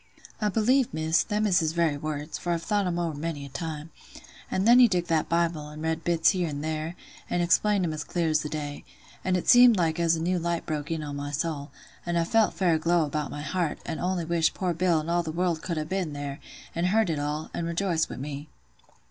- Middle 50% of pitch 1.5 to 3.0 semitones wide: Yes, narrow, 2.5 semitones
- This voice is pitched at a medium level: Yes, medium, 165 Hz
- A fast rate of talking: Yes, fast, 245 wpm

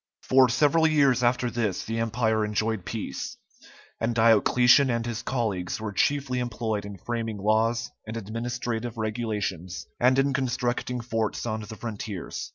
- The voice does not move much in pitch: Yes, narrow, 2.2 semitones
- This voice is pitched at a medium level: No, low, 115 Hz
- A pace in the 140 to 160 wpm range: Yes, average, 145 wpm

